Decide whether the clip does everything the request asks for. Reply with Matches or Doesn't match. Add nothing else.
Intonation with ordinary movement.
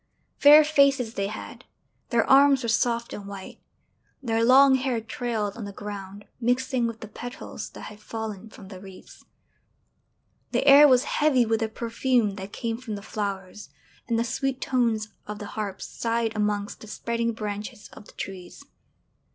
Matches